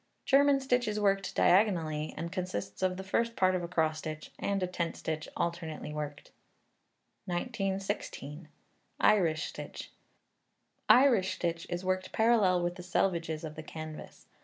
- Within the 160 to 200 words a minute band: No, average, 145 wpm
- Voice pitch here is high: No, medium, 180 Hz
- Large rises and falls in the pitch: No, average, 3.7 semitones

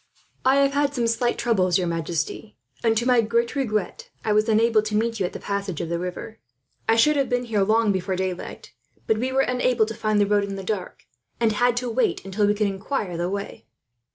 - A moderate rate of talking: No, fast, 230 wpm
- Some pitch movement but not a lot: Yes, average, 3.5 semitones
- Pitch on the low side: No, high, 215 Hz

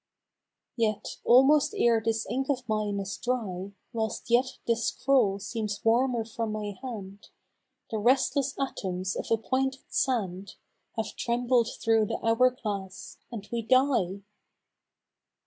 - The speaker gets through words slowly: Yes, slow, 130 wpm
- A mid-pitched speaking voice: No, high, 225 Hz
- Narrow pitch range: No, average, 3.5 semitones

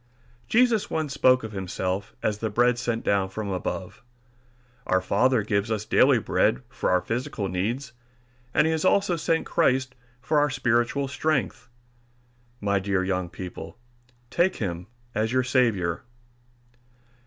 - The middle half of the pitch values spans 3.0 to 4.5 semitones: No, average, 5.3 semitones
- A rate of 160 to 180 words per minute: No, average, 145 wpm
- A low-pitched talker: Yes, low, 115 Hz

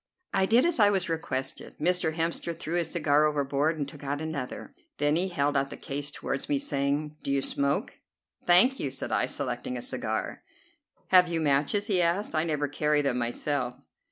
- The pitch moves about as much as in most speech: Yes, average, 3.5 semitones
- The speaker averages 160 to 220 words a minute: Yes, average, 190 wpm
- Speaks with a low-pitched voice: No, medium, 150 Hz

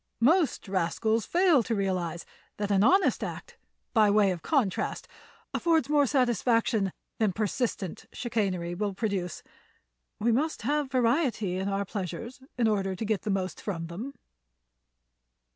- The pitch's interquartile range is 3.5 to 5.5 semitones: Yes, average, 4.6 semitones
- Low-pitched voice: No, high, 215 Hz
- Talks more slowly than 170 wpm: Yes, average, 140 wpm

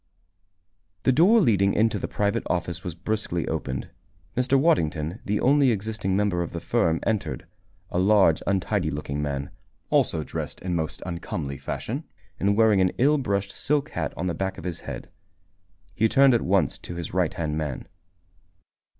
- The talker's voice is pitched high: No, very low, 95 Hz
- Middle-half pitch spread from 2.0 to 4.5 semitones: No, average, 4.9 semitones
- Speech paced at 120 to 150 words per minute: No, average, 165 wpm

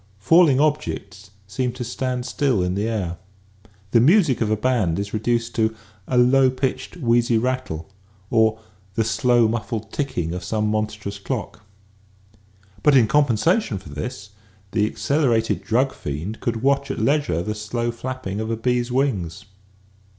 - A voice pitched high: No, low, 115 Hz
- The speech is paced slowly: No, average, 160 wpm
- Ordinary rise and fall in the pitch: Yes, average, 4.1 semitones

